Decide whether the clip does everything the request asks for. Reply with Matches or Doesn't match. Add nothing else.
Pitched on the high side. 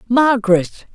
Matches